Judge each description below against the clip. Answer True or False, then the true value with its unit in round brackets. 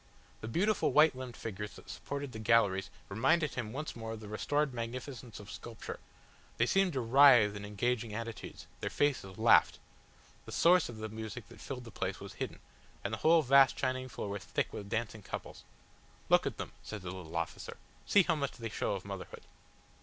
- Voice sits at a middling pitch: False (115 Hz)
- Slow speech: False (195 wpm)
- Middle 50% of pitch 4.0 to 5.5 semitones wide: True (4.4 semitones)